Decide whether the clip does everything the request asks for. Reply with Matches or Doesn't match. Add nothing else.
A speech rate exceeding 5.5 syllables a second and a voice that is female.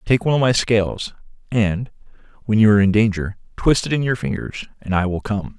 Doesn't match